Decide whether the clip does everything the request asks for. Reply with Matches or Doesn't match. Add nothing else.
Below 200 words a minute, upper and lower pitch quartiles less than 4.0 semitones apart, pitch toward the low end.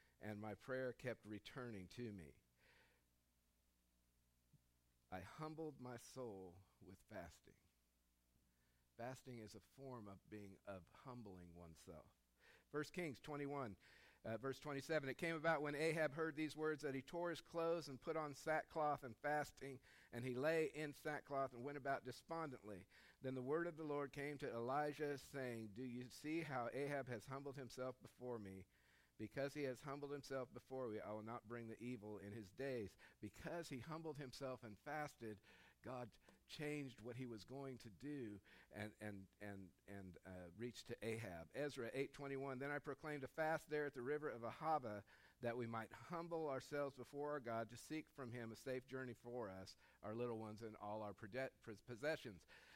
Doesn't match